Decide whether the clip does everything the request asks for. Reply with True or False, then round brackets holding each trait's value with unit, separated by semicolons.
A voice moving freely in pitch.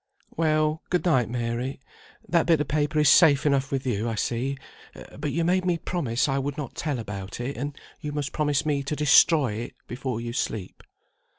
False (3.9 semitones)